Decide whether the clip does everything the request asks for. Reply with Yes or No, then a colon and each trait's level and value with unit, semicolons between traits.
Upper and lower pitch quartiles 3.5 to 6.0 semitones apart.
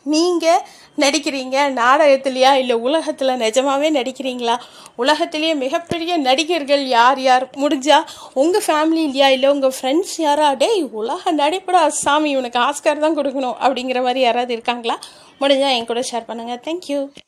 No: average, 3.1 semitones